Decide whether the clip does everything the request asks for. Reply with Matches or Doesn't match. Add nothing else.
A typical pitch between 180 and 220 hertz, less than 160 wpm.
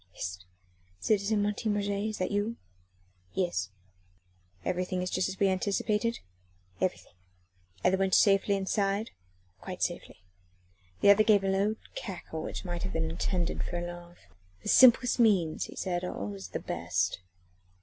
Matches